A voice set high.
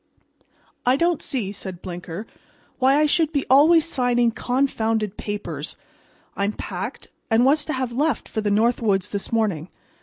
Yes: high, 235 Hz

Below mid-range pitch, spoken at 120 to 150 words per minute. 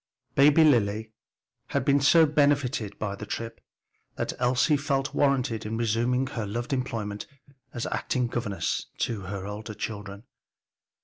Yes: low, 120 Hz; slow, 135 wpm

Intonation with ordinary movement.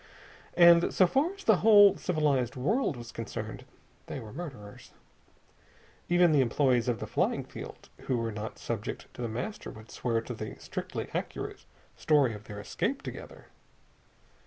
No: wide, 7.3 semitones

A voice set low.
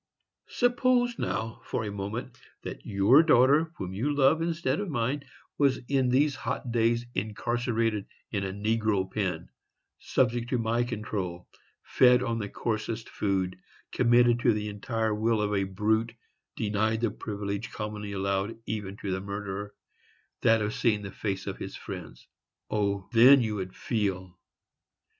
Yes: low, 110 Hz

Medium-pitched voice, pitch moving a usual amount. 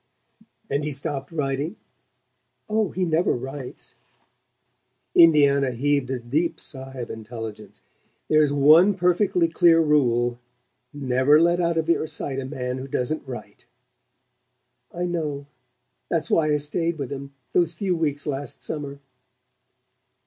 Yes: medium, 145 Hz; average, 3.7 semitones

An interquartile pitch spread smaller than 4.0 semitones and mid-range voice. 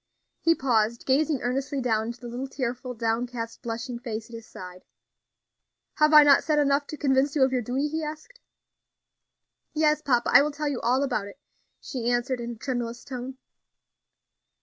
No: average, 3.2 semitones; very high, 255 Hz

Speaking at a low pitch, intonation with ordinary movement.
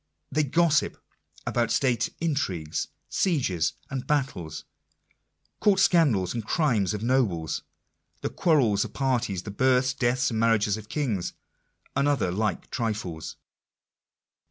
No: low, 120 Hz; wide, 5.7 semitones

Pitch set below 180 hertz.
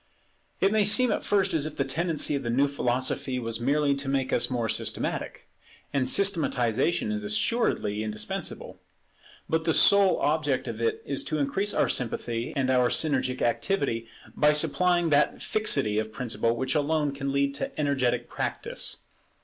Yes: medium, 140 Hz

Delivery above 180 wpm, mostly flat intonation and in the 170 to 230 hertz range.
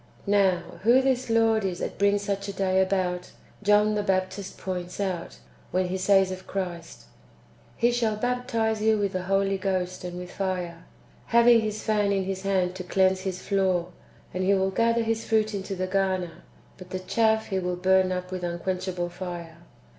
Yes: average, 190 wpm; narrow, 2.3 semitones; high, 190 Hz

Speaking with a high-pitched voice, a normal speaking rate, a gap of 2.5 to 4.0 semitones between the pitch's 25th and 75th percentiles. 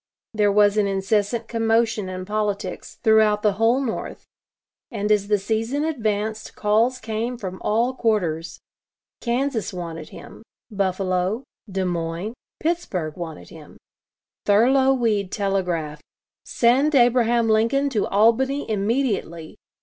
No: high, 215 Hz; slow, 120 wpm; average, 3.4 semitones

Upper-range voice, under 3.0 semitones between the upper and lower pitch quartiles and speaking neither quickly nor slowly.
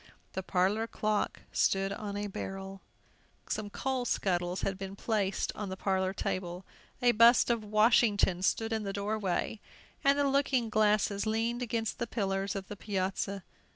Yes: high, 205 Hz; narrow, 2.6 semitones; average, 160 wpm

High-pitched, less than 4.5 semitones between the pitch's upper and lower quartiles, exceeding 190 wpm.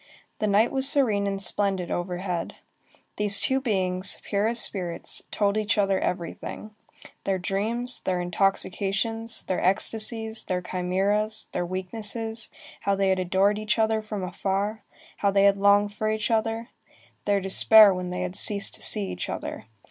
No: high, 200 Hz; average, 2.7 semitones; average, 155 wpm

